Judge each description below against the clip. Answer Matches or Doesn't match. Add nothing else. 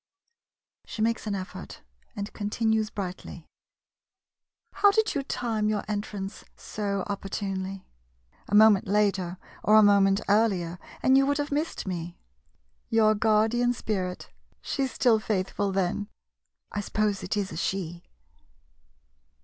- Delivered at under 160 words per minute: Matches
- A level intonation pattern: Matches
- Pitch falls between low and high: Doesn't match